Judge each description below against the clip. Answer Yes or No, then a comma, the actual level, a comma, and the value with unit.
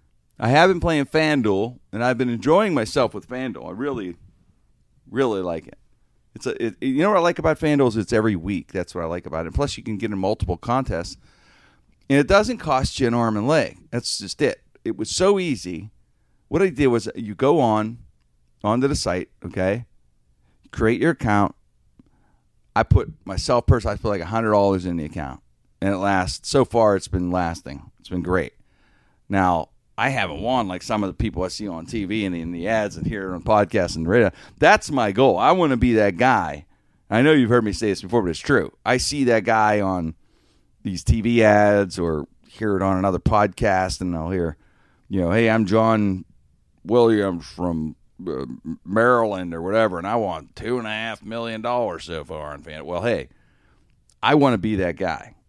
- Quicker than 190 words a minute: Yes, average, 200 wpm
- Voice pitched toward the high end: No, low, 100 Hz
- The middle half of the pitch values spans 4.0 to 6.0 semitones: Yes, average, 4.6 semitones